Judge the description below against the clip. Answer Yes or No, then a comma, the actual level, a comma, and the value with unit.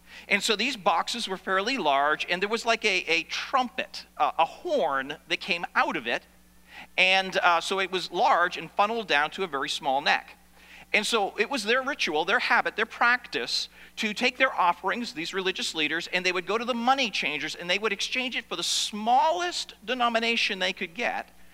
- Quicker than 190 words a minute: Yes, fast, 205 wpm